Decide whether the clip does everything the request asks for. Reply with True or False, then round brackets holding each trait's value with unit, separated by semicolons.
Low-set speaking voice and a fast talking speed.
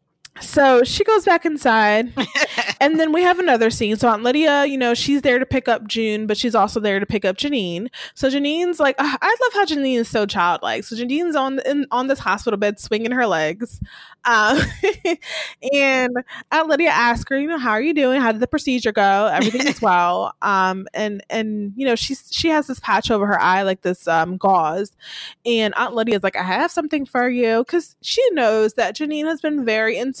False (245 Hz; 215 wpm)